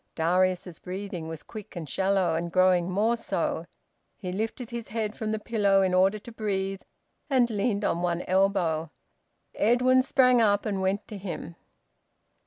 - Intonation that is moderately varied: Yes, average, 3.1 semitones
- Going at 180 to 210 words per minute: No, average, 160 wpm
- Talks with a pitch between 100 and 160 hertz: No, high, 195 Hz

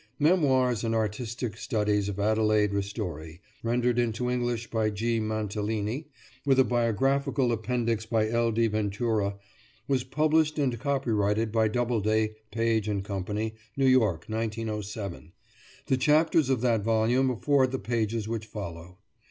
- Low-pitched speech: Yes, low, 115 Hz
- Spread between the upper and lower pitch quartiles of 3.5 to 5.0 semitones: No, average, 2.7 semitones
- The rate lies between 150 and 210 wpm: No, slow, 135 wpm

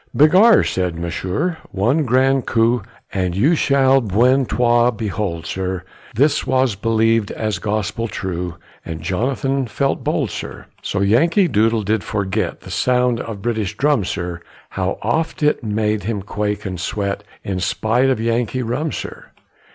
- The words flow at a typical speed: Yes, average, 145 wpm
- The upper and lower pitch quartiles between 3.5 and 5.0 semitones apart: Yes, average, 4.7 semitones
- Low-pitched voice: Yes, low, 110 Hz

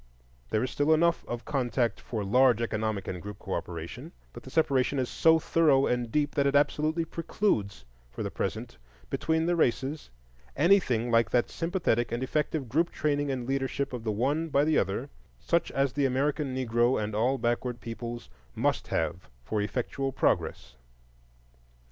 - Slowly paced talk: No, average, 165 wpm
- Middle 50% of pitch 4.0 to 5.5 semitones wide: Yes, average, 4.4 semitones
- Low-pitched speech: Yes, low, 130 Hz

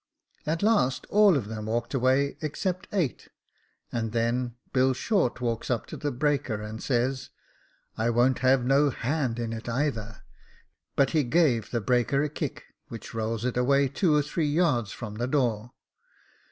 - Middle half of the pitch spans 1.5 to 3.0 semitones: No, average, 3.8 semitones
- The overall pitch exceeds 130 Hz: No, low, 125 Hz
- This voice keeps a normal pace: Yes, average, 170 wpm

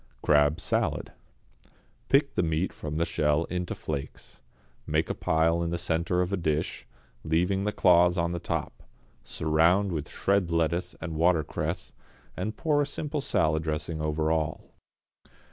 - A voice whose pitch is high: No, very low, 85 Hz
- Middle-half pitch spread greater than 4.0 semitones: No, narrow, 2.4 semitones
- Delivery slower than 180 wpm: Yes, average, 150 wpm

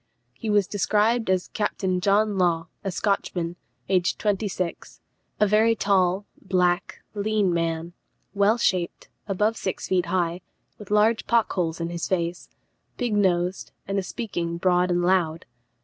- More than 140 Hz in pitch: Yes, high, 190 Hz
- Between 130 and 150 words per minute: Yes, average, 145 wpm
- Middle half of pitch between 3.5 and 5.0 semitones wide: No, average, 2.9 semitones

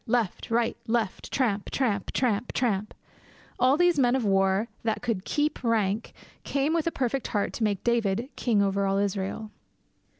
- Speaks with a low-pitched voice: No, high, 225 Hz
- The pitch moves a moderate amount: Yes, average, 4.0 semitones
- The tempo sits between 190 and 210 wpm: No, average, 165 wpm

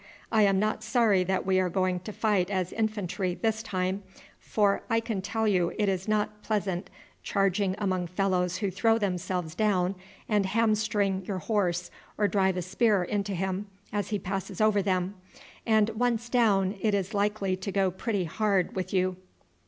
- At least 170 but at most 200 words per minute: Yes, average, 175 wpm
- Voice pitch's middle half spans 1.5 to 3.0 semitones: Yes, narrow, 2.5 semitones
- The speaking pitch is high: Yes, high, 195 Hz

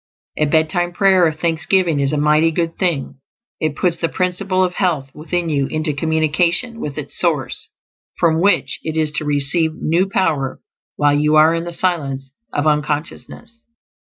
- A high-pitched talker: No, medium, 160 Hz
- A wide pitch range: No, average, 2.8 semitones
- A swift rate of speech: No, average, 165 wpm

